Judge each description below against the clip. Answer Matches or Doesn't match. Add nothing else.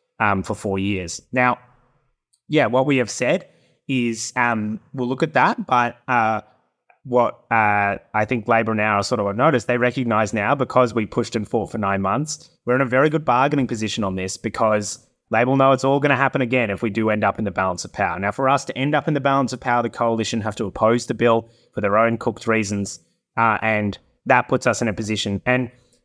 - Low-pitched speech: Matches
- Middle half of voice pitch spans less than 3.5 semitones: Matches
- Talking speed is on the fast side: Matches